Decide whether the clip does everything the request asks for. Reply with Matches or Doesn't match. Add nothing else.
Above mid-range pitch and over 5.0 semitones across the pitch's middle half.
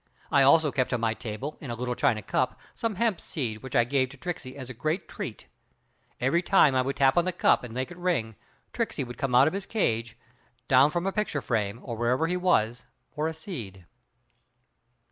Doesn't match